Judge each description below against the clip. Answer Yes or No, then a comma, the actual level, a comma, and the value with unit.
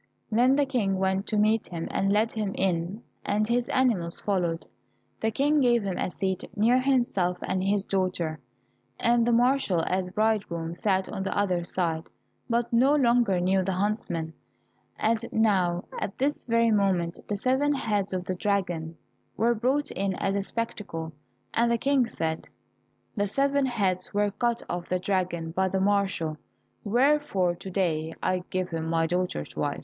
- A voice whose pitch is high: Yes, high, 200 Hz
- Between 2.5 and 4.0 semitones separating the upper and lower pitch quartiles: No, average, 4.5 semitones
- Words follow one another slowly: No, average, 170 wpm